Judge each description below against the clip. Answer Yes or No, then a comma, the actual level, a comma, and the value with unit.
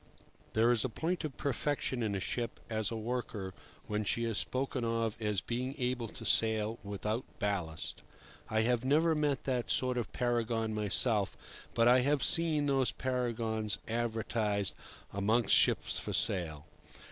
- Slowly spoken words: No, average, 155 wpm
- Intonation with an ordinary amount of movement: Yes, average, 3.0 semitones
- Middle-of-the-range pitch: No, low, 115 Hz